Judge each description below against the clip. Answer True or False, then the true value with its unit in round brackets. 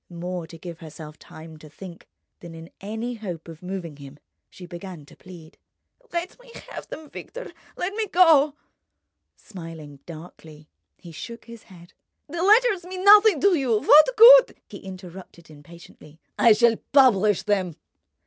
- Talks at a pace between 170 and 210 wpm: False (150 wpm)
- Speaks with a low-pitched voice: False (190 Hz)